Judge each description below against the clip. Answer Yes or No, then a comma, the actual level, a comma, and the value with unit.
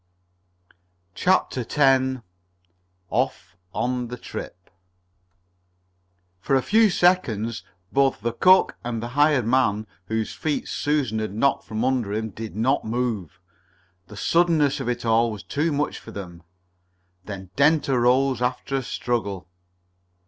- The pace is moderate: No, slow, 130 wpm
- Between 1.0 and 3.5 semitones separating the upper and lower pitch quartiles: No, average, 4.0 semitones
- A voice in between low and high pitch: No, low, 125 Hz